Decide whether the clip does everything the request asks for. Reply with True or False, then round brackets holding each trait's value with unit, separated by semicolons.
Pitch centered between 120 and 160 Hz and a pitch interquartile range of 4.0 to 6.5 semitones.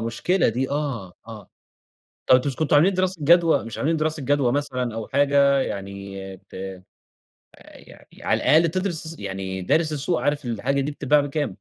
True (140 Hz; 5.2 semitones)